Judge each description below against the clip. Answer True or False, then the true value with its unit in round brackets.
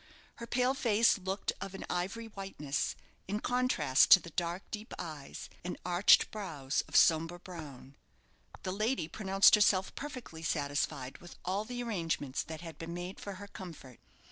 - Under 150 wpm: False (160 wpm)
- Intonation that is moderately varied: True (4.6 semitones)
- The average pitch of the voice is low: False (185 Hz)